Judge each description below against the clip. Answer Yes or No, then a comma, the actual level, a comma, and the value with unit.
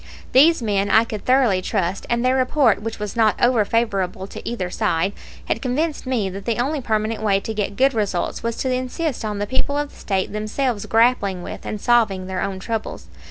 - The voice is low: No, high, 220 Hz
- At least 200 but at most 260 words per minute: Yes, fast, 205 wpm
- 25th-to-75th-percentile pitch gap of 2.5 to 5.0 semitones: Yes, average, 4.2 semitones